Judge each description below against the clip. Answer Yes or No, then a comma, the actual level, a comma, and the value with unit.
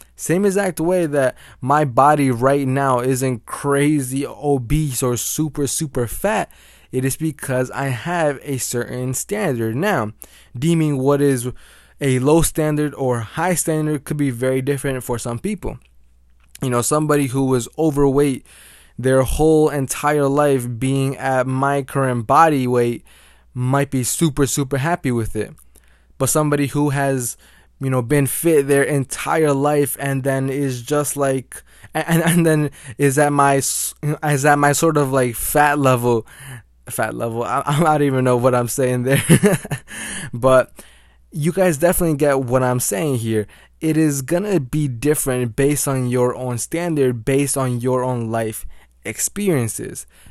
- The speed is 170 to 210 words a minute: No, average, 155 wpm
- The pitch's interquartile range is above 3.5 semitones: No, average, 3.0 semitones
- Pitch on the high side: No, low, 135 Hz